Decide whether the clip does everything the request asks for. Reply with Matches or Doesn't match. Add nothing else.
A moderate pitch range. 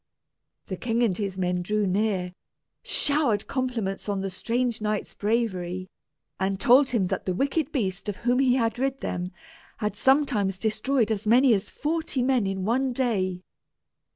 Matches